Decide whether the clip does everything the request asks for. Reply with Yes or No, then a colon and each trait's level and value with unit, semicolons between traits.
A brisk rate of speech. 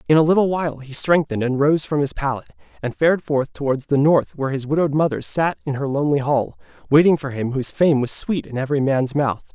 Yes: fast, 235 wpm